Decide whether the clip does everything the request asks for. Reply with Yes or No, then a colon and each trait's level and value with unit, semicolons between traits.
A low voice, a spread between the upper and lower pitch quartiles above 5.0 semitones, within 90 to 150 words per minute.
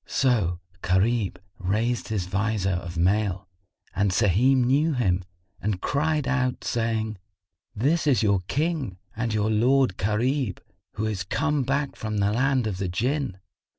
Yes: low, 110 Hz; wide, 5.4 semitones; average, 145 wpm